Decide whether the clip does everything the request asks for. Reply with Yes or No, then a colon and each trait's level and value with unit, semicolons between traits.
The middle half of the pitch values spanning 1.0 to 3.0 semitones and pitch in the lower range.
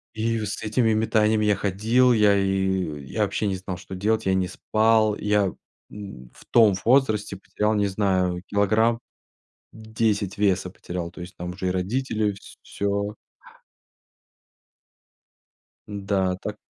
Yes: narrow, 2.5 semitones; low, 100 Hz